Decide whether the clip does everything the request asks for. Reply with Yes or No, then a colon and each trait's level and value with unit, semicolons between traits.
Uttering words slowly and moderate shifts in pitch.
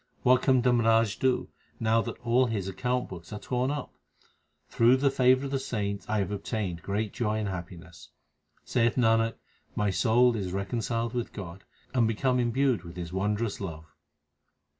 No: average, 165 wpm; average, 3.9 semitones